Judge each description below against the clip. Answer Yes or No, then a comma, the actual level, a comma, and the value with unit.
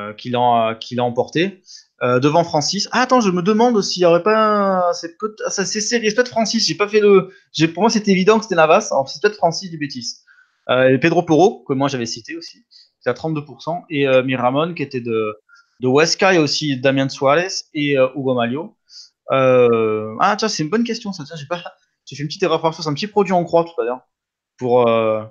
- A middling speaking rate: No, fast, 230 wpm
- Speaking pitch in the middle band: Yes, medium, 165 Hz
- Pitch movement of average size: No, wide, 7.5 semitones